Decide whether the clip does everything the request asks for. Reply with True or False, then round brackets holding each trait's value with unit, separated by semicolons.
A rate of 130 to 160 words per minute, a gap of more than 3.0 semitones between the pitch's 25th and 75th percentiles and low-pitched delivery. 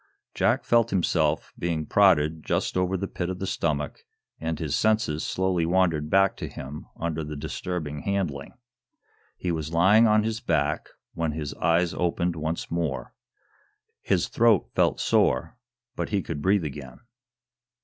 True (150 wpm; 3.8 semitones; 85 Hz)